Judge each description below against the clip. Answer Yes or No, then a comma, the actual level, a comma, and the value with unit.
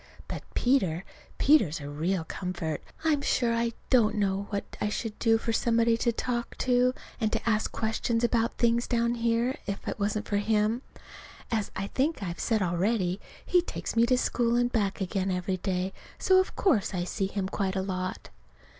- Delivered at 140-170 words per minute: No, average, 180 wpm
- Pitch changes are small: No, average, 3.7 semitones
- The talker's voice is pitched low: No, high, 220 Hz